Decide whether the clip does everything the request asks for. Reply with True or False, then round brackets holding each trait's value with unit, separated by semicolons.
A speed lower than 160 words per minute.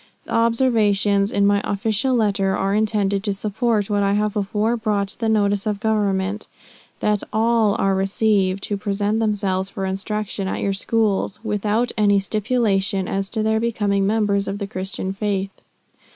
False (165 wpm)